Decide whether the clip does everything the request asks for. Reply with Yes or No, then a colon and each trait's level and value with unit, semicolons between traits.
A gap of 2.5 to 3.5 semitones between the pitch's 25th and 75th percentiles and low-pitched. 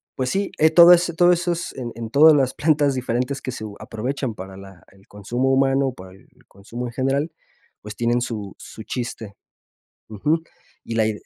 No: average, 4.7 semitones; low, 125 Hz